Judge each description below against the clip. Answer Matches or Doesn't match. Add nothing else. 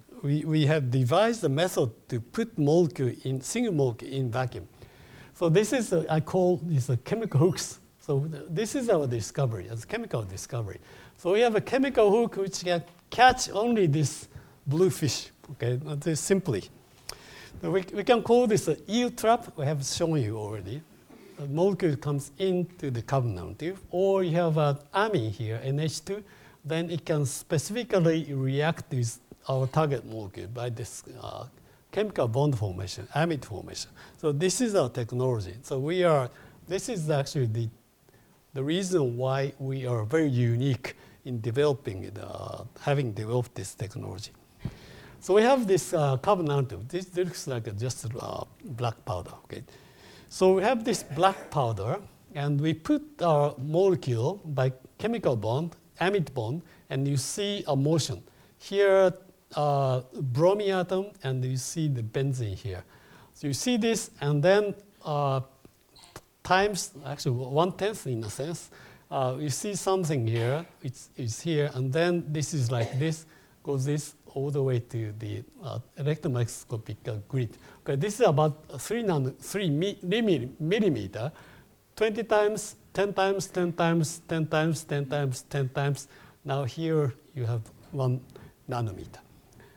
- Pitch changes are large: Matches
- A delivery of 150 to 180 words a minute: Matches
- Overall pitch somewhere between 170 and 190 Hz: Doesn't match